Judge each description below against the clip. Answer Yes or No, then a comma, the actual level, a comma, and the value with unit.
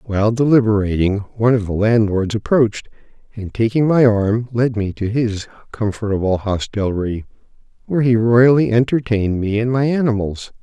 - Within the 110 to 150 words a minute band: Yes, average, 140 wpm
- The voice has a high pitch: No, low, 110 Hz